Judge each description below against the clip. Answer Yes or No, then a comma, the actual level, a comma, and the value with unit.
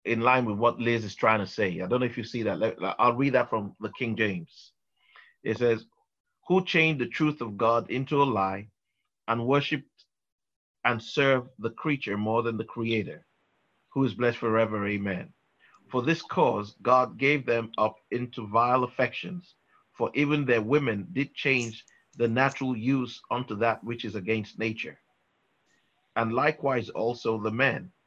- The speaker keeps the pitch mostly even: No, average, 3.1 semitones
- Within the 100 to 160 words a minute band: No, average, 170 wpm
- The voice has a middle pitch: No, low, 120 Hz